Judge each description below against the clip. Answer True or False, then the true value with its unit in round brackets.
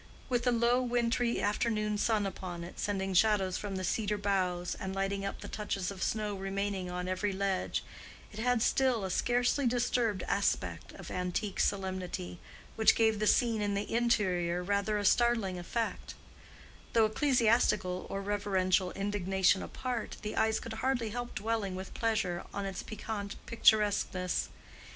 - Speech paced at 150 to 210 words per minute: True (155 wpm)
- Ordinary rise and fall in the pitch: True (3.1 semitones)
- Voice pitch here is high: True (205 Hz)